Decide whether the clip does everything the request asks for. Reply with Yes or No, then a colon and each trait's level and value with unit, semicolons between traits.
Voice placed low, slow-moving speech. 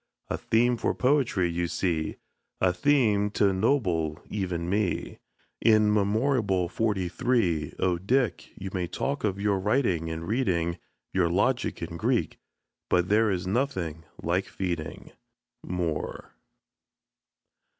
Yes: very low, 95 Hz; slow, 125 wpm